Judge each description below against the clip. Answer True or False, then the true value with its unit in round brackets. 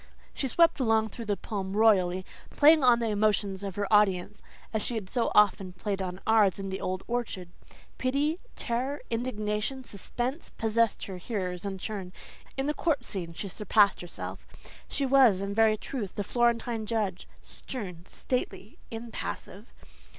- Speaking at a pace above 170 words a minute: False (160 wpm)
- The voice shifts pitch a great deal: False (3.7 semitones)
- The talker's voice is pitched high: True (215 Hz)